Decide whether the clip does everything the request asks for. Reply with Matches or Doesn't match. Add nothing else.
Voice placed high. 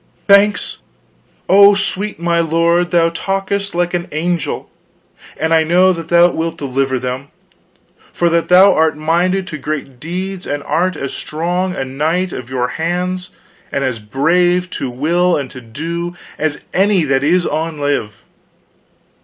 Doesn't match